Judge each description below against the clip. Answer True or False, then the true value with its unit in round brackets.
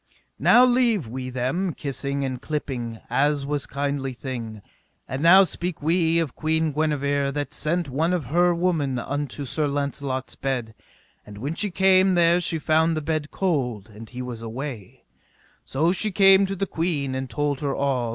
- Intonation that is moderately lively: True (4.2 semitones)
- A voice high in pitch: False (145 Hz)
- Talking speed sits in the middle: True (170 wpm)